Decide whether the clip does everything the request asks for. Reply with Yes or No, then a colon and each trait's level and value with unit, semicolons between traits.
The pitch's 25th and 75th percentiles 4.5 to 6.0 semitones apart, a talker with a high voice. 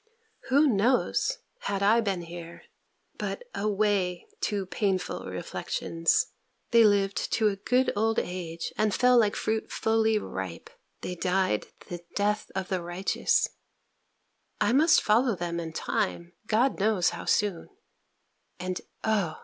No: average, 3.7 semitones; high, 200 Hz